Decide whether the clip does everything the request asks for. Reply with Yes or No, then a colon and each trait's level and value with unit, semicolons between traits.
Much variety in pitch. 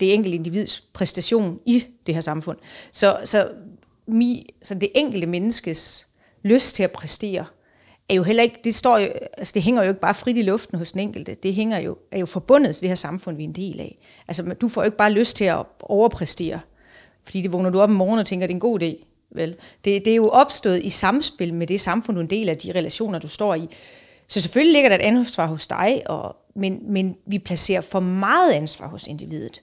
No: average, 4.0 semitones